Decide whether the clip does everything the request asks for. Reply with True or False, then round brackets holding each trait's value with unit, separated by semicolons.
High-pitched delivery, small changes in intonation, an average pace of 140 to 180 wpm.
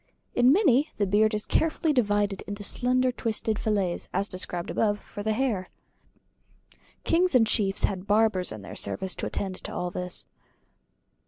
False (210 Hz; 4.3 semitones; 160 wpm)